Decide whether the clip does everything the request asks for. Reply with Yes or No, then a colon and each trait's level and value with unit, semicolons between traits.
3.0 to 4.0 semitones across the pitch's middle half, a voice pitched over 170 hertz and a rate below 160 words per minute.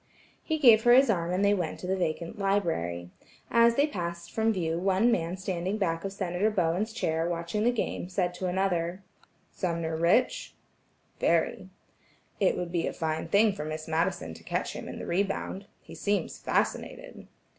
No: average, 3.5 semitones; medium, 185 Hz; average, 175 wpm